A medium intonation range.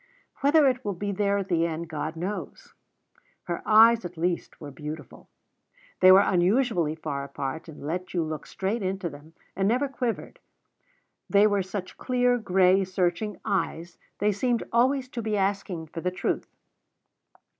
Yes: average, 4.2 semitones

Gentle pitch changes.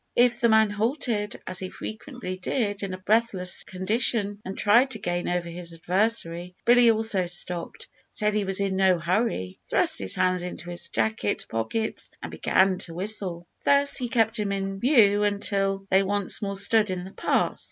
No: average, 3.3 semitones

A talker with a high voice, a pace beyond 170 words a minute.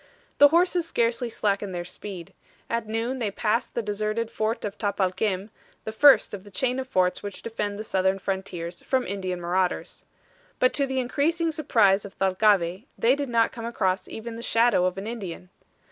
Yes: high, 215 Hz; average, 180 wpm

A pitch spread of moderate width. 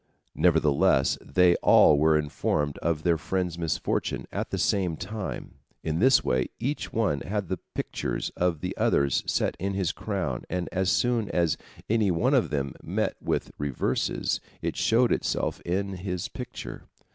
Yes: average, 4.3 semitones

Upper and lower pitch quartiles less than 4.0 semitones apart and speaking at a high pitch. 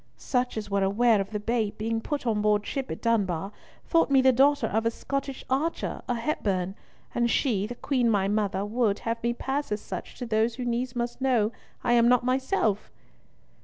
Yes: average, 3.4 semitones; high, 235 Hz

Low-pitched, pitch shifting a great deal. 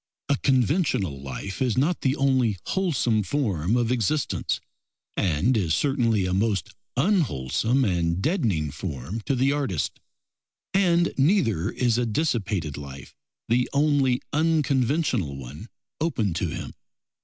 Yes: low, 115 Hz; wide, 7.5 semitones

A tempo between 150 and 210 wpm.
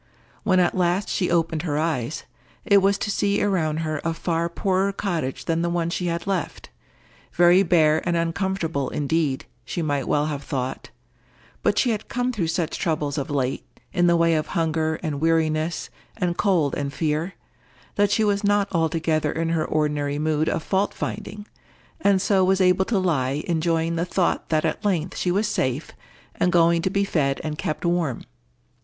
Yes: average, 180 wpm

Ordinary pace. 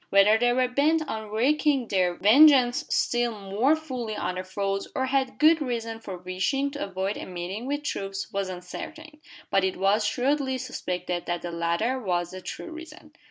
Yes: average, 180 wpm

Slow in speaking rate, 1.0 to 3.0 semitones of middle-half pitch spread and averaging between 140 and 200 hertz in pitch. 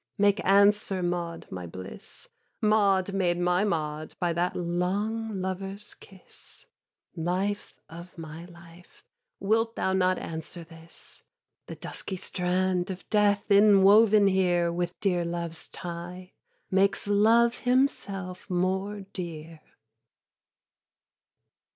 Yes: slow, 110 wpm; average, 2.7 semitones; medium, 185 Hz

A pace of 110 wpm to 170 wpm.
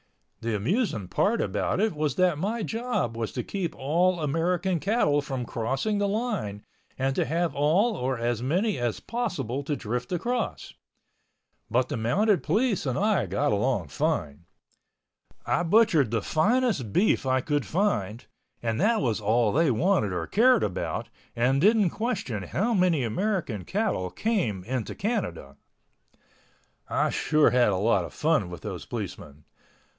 Yes: average, 155 wpm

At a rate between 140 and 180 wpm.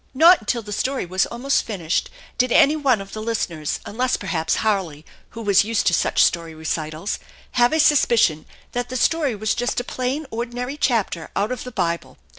No: average, 200 wpm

